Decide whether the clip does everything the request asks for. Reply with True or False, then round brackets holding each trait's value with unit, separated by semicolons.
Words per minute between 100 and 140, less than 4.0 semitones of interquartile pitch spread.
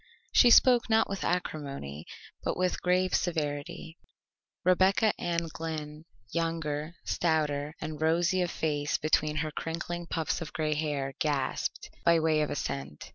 True (135 wpm; 2.7 semitones)